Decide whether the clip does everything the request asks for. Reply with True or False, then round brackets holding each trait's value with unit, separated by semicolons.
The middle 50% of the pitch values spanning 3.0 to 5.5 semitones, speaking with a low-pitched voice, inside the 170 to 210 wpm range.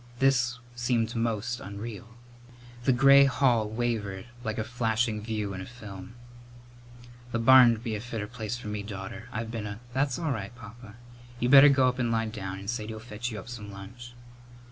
False (2.5 semitones; 115 Hz; 190 wpm)